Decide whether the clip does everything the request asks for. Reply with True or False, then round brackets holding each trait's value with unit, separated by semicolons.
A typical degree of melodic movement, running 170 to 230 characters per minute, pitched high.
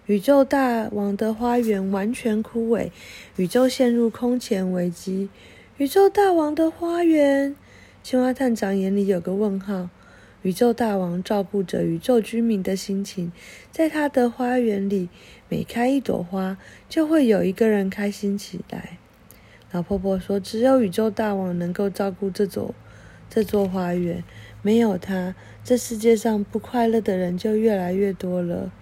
True (4.0 semitones; 225 characters per minute; 205 Hz)